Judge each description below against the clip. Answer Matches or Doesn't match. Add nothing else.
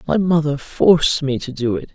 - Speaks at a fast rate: Matches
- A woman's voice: Doesn't match